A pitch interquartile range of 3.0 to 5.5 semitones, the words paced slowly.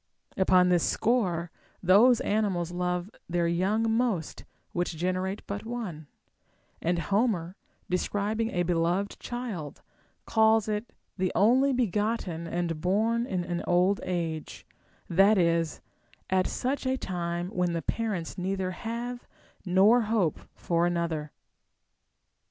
Yes: average, 4.2 semitones; slow, 120 wpm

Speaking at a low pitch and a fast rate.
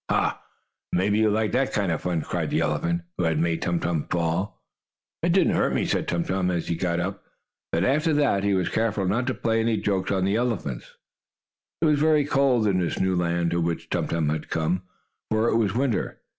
Yes: very low, 95 Hz; fast, 220 wpm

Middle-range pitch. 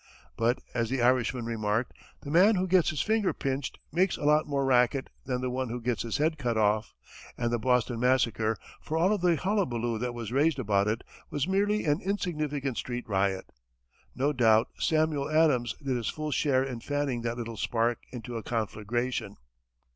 No: low, 125 Hz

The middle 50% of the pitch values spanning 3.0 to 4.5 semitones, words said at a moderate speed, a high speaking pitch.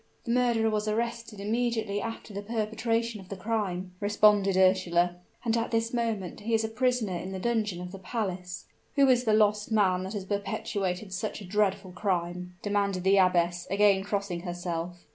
Yes: average, 3.3 semitones; average, 180 wpm; high, 205 Hz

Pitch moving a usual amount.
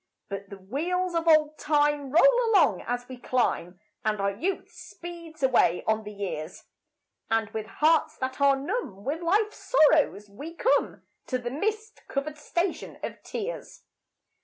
No: wide, 7.7 semitones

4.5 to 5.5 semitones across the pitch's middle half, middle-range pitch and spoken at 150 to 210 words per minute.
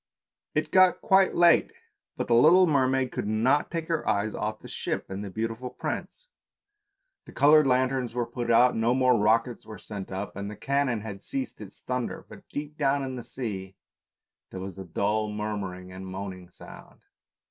No: average, 4.9 semitones; low, 115 Hz; average, 190 wpm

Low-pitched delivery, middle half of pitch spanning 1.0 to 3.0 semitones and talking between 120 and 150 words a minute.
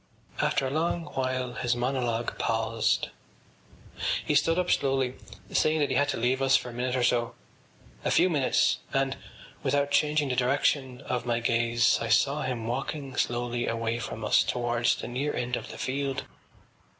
No: low, 125 Hz; average, 2.7 semitones; average, 175 wpm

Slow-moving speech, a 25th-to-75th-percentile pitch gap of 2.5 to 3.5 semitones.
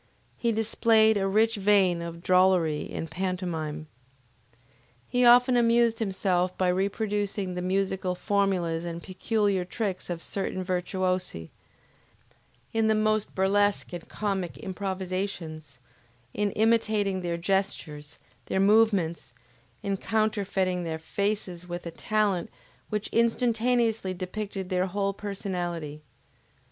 Yes: slow, 110 wpm; average, 3.0 semitones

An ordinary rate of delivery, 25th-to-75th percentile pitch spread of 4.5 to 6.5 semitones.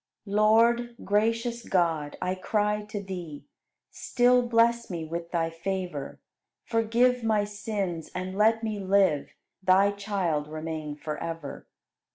No: slow, 125 wpm; average, 5.0 semitones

